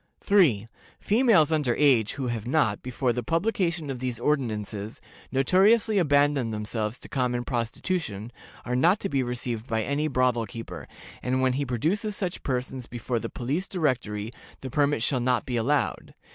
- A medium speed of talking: Yes, average, 160 wpm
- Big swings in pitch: No, average, 4.4 semitones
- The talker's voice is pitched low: Yes, low, 130 Hz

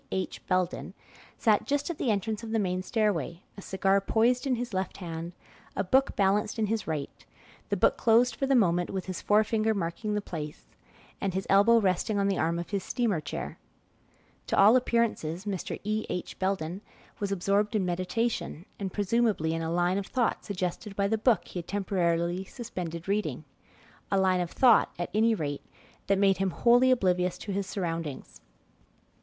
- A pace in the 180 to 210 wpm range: Yes, average, 185 wpm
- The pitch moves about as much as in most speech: Yes, average, 3.6 semitones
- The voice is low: No, high, 195 Hz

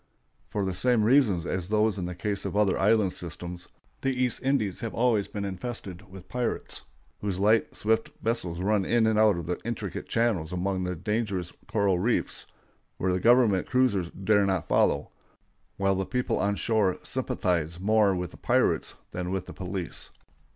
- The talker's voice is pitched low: Yes, low, 100 Hz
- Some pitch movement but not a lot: Yes, average, 3.5 semitones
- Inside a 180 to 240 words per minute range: No, average, 170 wpm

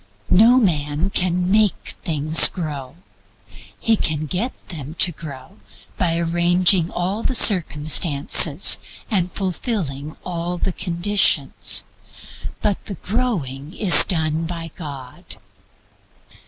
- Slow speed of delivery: Yes, slow, 105 wpm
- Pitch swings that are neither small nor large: Yes, average, 3.9 semitones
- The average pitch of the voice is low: No, medium, 170 Hz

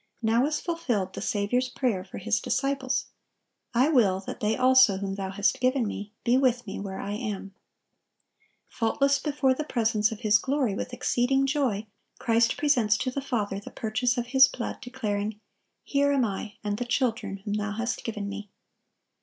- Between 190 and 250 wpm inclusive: No, average, 180 wpm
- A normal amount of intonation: Yes, average, 4.1 semitones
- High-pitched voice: Yes, high, 230 Hz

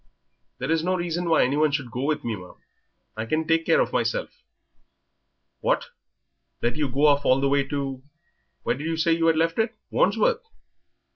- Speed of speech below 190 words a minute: No, average, 195 wpm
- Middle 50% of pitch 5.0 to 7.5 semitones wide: No, average, 3.4 semitones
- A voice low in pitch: No, medium, 155 Hz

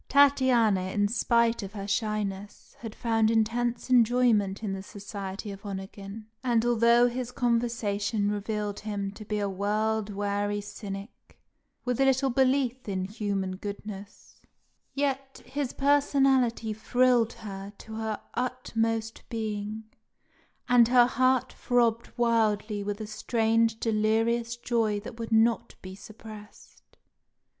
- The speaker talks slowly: Yes, slow, 125 wpm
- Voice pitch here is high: Yes, high, 220 Hz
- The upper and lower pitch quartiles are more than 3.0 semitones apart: No, average, 2.7 semitones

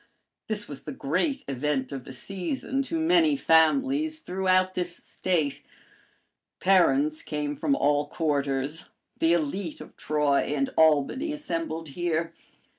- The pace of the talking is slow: Yes, slow, 125 wpm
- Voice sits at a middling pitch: Yes, medium, 165 Hz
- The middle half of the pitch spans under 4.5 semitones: No, average, 5.3 semitones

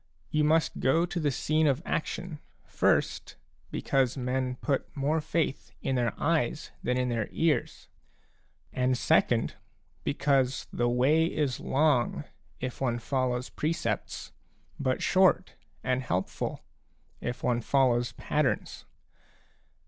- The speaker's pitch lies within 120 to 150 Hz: Yes, low, 135 Hz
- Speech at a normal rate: No, slow, 125 wpm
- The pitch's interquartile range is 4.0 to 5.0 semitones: No, average, 3.6 semitones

